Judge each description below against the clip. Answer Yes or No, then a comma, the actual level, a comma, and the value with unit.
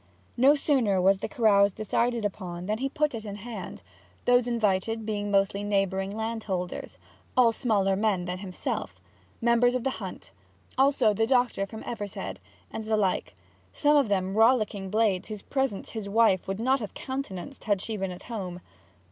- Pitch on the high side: Yes, high, 215 Hz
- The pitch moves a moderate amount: Yes, average, 3.6 semitones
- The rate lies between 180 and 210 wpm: No, average, 170 wpm